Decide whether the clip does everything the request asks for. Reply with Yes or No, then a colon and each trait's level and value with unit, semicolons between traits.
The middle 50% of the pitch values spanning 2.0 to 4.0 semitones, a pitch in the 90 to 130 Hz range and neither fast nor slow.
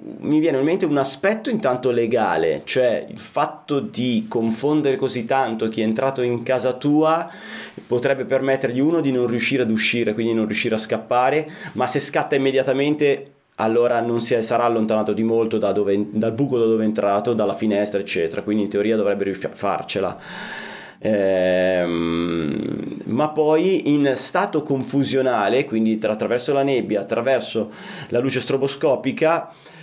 No: average, 4.4 semitones; low, 125 Hz; average, 155 wpm